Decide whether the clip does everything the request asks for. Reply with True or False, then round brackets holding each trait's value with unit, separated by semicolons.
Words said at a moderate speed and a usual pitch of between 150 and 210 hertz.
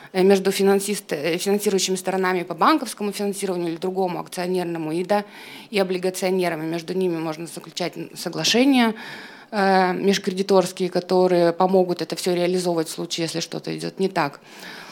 True (125 wpm; 185 Hz)